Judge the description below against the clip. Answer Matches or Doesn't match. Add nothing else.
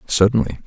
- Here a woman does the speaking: Doesn't match